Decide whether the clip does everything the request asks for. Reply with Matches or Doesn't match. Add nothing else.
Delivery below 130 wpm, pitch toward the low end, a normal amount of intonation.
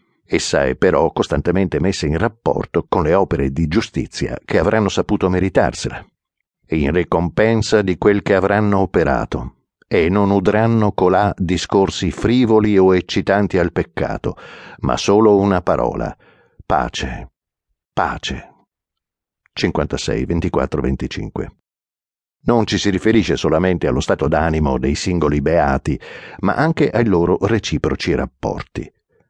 Matches